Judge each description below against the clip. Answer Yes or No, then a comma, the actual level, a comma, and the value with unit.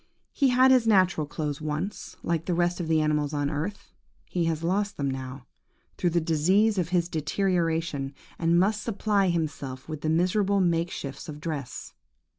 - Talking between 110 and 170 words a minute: No, average, 180 wpm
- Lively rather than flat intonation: No, average, 3.9 semitones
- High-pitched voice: No, medium, 165 Hz